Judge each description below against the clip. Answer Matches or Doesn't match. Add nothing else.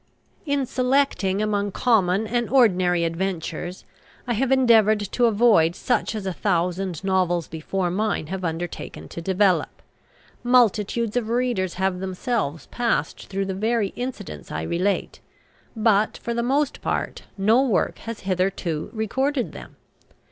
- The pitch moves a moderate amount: Matches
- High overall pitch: Matches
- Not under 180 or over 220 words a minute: Doesn't match